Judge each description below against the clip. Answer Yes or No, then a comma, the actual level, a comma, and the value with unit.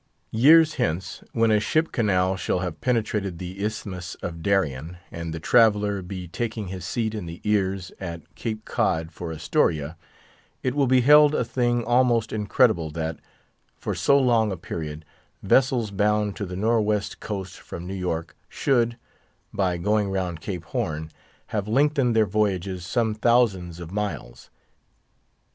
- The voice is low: Yes, low, 100 Hz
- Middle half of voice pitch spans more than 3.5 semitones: Yes, average, 4.6 semitones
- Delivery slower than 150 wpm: No, average, 155 wpm